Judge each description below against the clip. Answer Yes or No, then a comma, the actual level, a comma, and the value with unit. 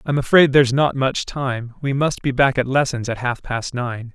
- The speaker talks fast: Yes, fast, 230 wpm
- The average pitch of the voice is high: No, low, 130 Hz